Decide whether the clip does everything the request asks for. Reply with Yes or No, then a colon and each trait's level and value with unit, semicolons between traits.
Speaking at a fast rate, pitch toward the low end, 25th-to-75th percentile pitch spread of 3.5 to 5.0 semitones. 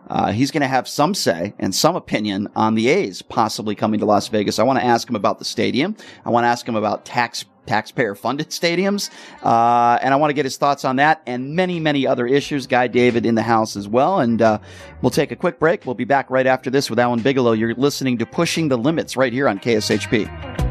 Yes: fast, 245 wpm; low, 125 Hz; average, 3.9 semitones